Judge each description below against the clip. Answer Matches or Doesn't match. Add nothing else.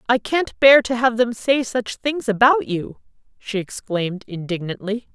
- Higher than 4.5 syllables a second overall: Doesn't match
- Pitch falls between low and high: Doesn't match